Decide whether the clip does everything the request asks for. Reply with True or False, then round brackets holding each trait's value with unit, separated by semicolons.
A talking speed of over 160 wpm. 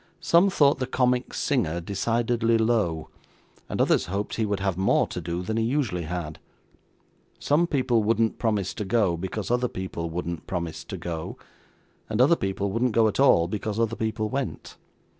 True (175 wpm)